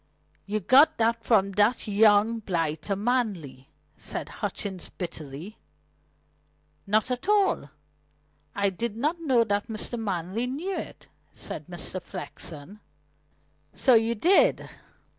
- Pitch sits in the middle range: No, high, 215 Hz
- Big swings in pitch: No, average, 4.0 semitones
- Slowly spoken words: Yes, slow, 115 wpm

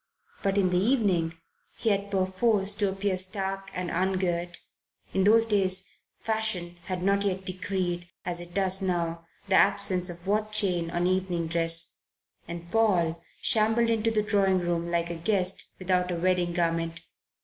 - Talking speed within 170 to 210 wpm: No, average, 155 wpm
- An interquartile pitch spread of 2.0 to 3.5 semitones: Yes, narrow, 2.6 semitones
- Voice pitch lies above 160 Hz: Yes, medium, 185 Hz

